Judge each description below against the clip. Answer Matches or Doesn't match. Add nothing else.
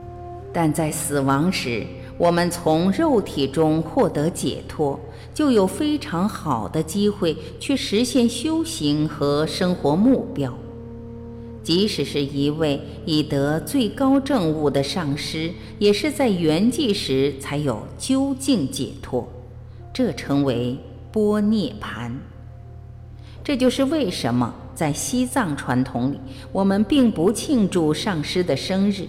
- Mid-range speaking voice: Matches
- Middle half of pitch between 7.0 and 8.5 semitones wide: Matches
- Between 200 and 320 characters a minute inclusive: Doesn't match